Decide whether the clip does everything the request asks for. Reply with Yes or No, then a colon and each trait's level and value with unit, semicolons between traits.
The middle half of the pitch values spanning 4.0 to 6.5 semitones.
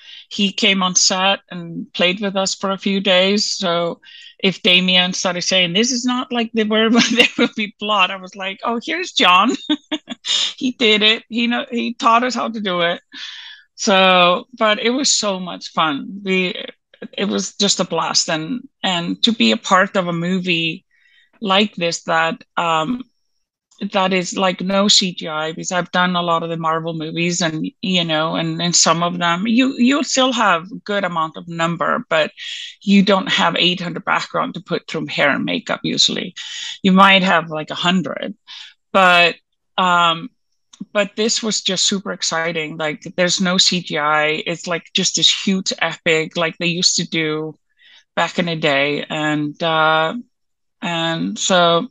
Yes: average, 5.1 semitones